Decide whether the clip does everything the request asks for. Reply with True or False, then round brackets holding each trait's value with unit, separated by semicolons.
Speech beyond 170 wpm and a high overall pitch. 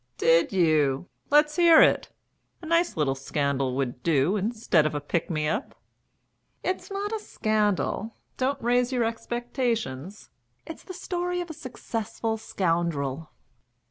False (140 wpm; 215 Hz)